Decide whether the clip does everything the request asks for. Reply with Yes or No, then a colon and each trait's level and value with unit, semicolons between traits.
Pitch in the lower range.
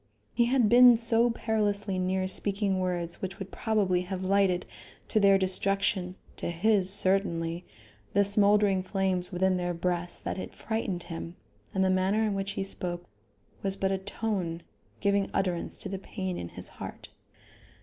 No: high, 195 Hz